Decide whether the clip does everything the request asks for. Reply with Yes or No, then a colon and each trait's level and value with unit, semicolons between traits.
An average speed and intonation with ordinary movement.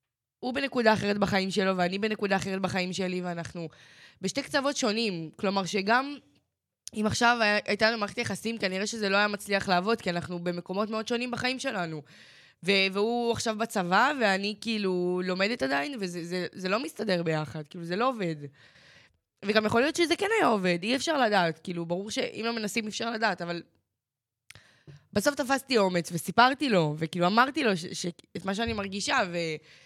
No: fast, 175 wpm; average, 4.4 semitones